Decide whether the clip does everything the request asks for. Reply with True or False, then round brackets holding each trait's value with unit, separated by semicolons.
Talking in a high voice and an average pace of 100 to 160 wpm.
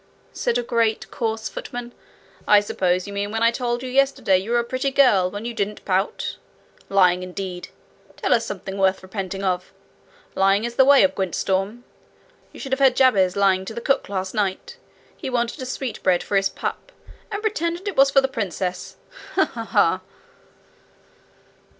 False (215 Hz; 180 wpm)